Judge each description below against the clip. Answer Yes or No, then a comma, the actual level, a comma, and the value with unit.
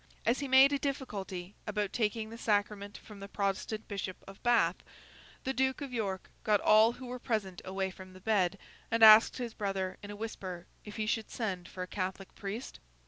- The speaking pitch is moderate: No, high, 210 Hz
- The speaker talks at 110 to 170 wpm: No, average, 195 wpm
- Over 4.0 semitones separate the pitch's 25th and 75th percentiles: No, average, 3.1 semitones